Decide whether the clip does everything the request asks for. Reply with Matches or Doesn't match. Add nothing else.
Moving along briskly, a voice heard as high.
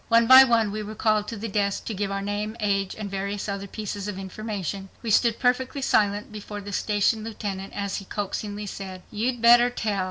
Matches